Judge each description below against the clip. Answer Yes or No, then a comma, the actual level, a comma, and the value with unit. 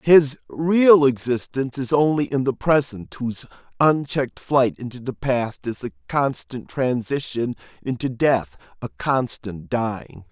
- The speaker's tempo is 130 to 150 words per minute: Yes, slow, 135 wpm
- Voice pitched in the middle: No, low, 130 Hz